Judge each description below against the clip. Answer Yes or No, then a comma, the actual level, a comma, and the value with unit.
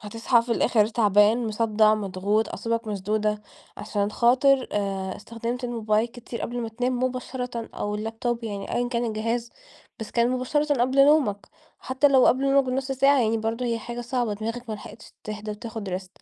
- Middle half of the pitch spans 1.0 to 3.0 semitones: Yes, narrow, 2.6 semitones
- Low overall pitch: No, high, 230 Hz